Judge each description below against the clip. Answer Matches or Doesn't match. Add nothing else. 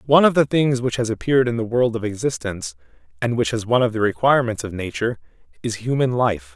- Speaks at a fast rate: Matches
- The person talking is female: Doesn't match